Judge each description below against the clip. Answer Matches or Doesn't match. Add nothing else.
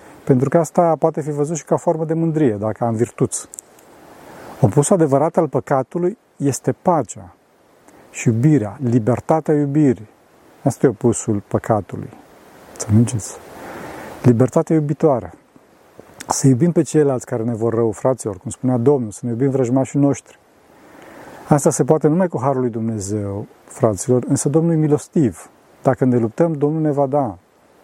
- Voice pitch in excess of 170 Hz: Doesn't match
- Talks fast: Doesn't match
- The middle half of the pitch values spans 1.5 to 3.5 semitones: Doesn't match